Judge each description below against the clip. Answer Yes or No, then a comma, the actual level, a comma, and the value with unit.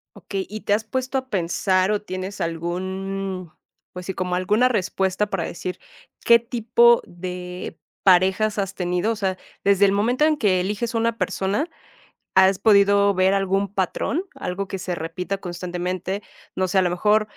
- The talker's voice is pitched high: Yes, high, 195 Hz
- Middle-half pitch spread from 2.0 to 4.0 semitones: Yes, narrow, 2.5 semitones